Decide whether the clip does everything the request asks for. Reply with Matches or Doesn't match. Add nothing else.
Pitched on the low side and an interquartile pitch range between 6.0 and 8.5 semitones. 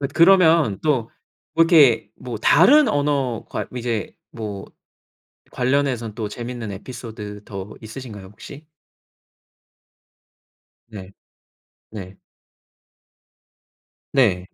Doesn't match